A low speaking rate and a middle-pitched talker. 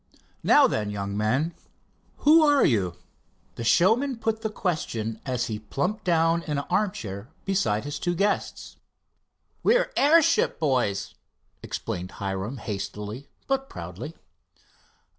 Yes: slow, 125 wpm; medium, 145 Hz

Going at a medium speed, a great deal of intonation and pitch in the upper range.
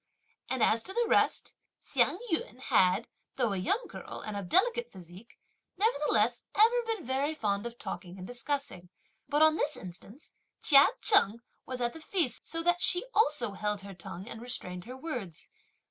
Yes: average, 175 wpm; wide, 7.9 semitones; high, 245 Hz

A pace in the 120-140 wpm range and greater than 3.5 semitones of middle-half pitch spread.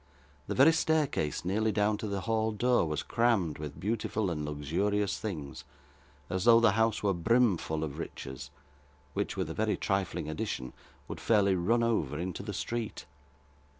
No: average, 160 wpm; wide, 5.4 semitones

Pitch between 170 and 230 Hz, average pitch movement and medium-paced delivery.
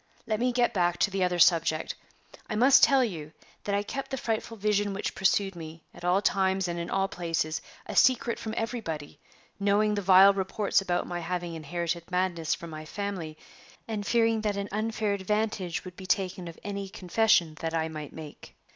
Yes: high, 190 Hz; average, 3.6 semitones; average, 190 wpm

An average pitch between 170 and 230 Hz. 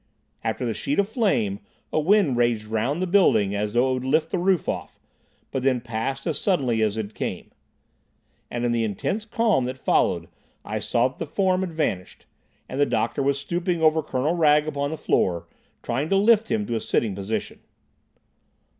No: medium, 140 Hz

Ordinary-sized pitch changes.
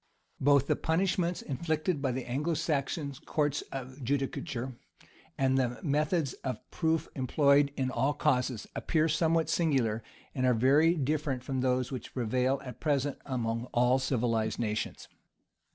Yes: average, 3.3 semitones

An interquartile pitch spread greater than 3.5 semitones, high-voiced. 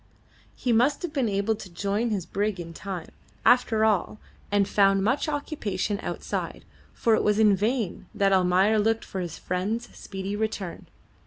No: narrow, 2.6 semitones; high, 205 Hz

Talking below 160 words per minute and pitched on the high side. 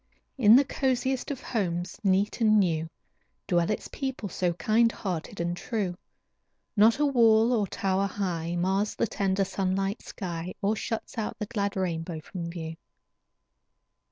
Yes: average, 150 wpm; high, 195 Hz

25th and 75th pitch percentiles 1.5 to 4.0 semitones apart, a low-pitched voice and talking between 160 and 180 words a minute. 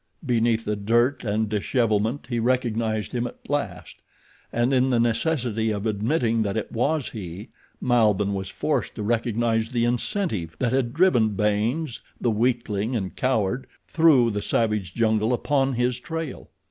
No: average, 2.9 semitones; low, 115 Hz; average, 150 wpm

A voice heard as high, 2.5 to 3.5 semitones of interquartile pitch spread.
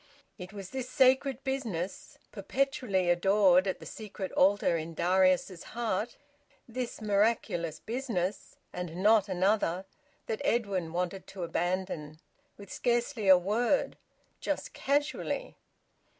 No: high, 200 Hz; average, 4.8 semitones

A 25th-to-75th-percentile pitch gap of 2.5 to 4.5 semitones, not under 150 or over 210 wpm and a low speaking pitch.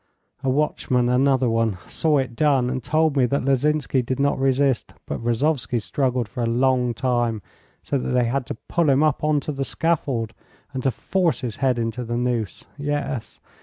Yes: average, 2.8 semitones; average, 190 wpm; low, 130 Hz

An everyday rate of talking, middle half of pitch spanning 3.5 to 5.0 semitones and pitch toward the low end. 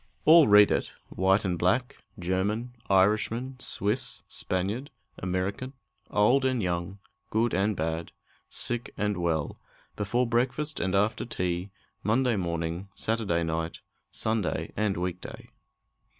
No: slow, 120 wpm; average, 4.7 semitones; low, 100 Hz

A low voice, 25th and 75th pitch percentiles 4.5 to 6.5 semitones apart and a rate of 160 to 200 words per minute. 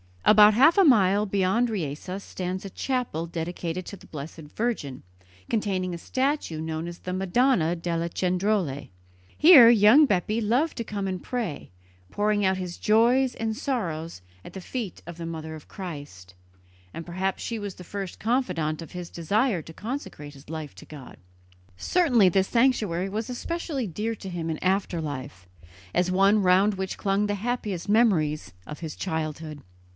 No: high, 190 Hz; average, 5.0 semitones; average, 165 wpm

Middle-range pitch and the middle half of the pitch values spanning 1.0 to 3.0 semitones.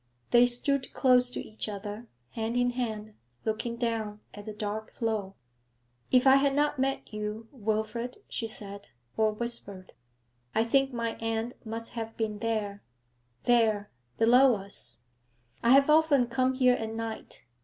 No: high, 225 Hz; narrow, 2.5 semitones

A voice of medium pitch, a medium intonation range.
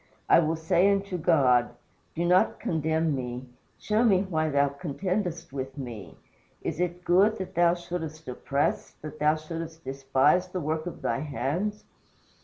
Yes: medium, 160 Hz; average, 4.1 semitones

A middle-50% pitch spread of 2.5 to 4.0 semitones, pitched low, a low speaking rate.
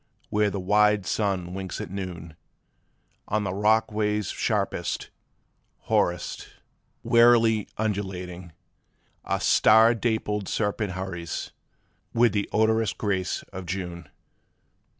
Yes: average, 2.9 semitones; low, 100 Hz; slow, 105 wpm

